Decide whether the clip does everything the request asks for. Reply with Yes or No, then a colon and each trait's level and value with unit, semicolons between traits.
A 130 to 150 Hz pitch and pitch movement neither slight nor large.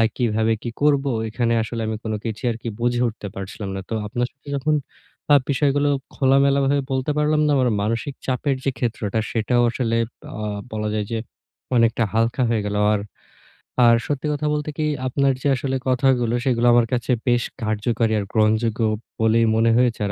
No: low, 120 Hz; average, 3.3 semitones